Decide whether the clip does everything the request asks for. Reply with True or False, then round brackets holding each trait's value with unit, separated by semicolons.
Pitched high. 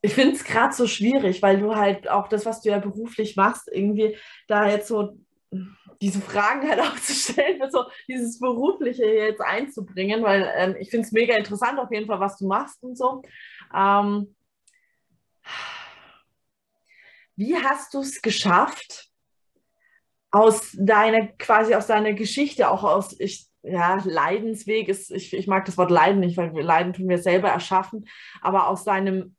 True (210 Hz)